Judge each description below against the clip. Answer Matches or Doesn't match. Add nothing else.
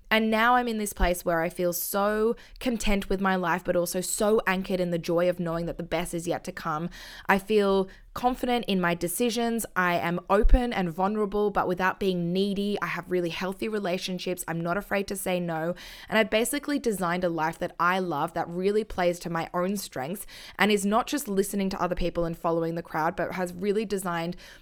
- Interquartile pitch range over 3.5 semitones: Doesn't match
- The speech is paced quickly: Matches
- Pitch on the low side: Doesn't match